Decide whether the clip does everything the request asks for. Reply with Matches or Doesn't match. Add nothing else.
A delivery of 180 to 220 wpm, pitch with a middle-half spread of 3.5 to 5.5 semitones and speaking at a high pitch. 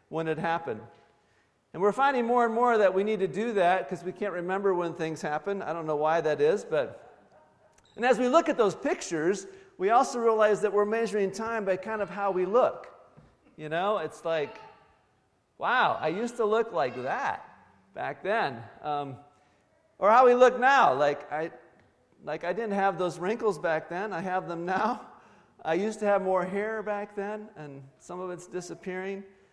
Matches